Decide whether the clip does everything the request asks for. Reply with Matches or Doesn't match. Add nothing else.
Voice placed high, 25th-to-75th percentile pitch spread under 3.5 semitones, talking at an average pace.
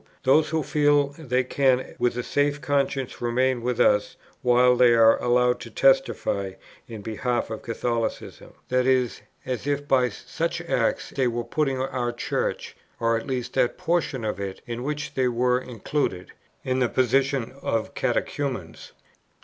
Doesn't match